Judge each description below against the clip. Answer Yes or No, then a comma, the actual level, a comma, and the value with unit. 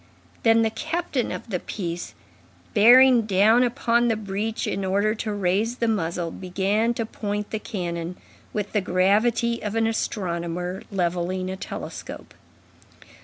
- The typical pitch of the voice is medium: No, high, 205 Hz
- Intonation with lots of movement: No, average, 3.6 semitones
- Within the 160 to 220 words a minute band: No, average, 140 wpm